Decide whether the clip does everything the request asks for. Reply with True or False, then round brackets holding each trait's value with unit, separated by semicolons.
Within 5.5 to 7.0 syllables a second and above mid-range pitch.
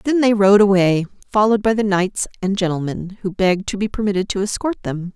True (6.0 syllables/s; 200 Hz)